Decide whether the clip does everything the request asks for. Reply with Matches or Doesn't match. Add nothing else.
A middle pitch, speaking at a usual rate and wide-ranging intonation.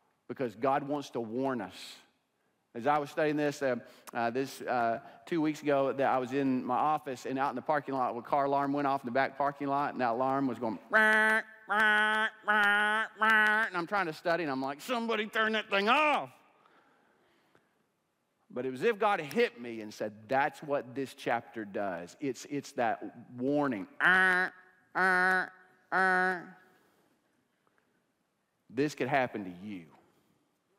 Matches